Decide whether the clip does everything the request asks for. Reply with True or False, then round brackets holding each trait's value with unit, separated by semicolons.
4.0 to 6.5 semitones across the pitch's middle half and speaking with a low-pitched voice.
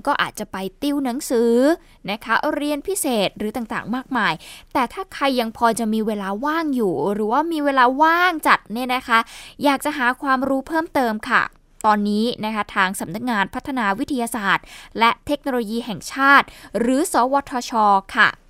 False (4.5 semitones; 245 Hz)